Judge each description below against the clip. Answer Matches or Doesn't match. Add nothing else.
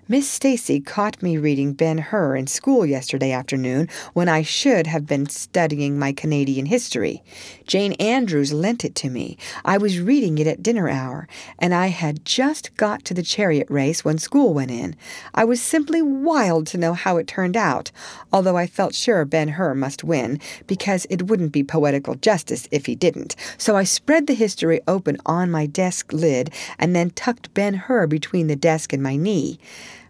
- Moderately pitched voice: Matches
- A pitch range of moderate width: Doesn't match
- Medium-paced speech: Matches